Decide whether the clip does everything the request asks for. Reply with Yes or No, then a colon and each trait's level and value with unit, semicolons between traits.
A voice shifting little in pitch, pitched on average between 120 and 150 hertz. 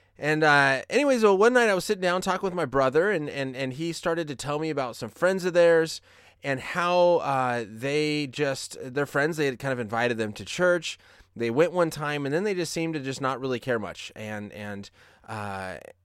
No: wide, 5.9 semitones; medium, 140 Hz